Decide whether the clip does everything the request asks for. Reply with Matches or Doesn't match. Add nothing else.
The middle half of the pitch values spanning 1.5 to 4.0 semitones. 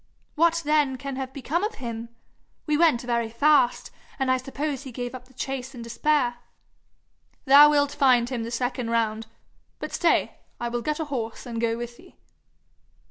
Matches